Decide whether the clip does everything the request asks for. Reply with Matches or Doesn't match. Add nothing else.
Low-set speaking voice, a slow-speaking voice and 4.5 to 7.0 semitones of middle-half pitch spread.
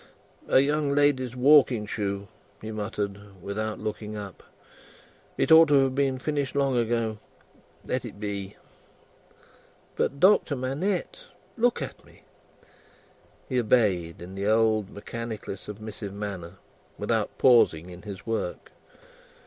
Matches